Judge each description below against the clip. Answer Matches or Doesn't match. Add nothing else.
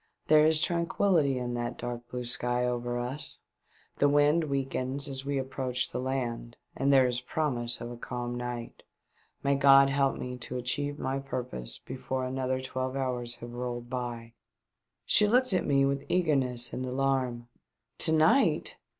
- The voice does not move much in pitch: Matches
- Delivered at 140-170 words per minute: Matches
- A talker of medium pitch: Doesn't match